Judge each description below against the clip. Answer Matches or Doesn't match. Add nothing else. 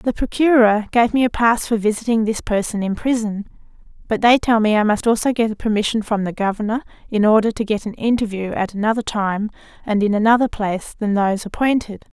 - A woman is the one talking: Matches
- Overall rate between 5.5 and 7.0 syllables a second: Matches